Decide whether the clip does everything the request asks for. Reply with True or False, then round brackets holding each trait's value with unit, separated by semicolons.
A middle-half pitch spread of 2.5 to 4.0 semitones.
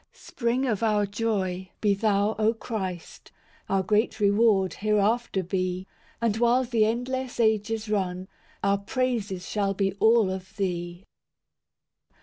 True (3.0 semitones)